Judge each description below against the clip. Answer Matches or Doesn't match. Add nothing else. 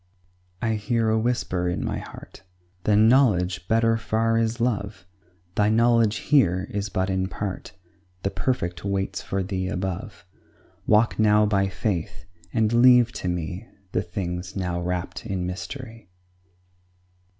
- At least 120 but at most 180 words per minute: Matches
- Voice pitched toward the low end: Matches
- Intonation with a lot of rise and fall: Doesn't match